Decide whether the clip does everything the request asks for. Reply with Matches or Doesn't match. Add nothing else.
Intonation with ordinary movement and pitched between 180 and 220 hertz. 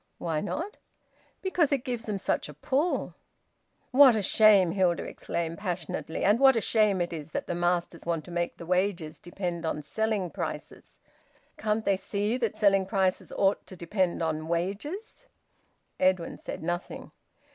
Matches